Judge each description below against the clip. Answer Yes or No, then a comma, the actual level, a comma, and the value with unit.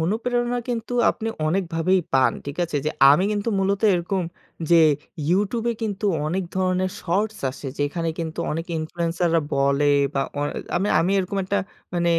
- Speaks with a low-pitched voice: No, medium, 180 Hz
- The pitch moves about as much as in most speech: Yes, average, 3.6 semitones